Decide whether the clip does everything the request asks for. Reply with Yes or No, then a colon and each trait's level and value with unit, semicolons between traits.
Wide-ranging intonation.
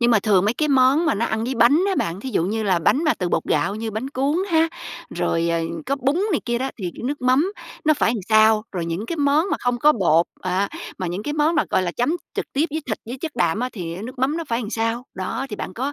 Yes: wide, 6.0 semitones